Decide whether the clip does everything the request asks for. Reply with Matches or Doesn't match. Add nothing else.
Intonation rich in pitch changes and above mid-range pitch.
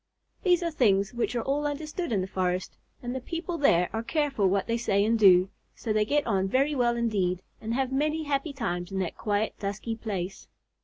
Matches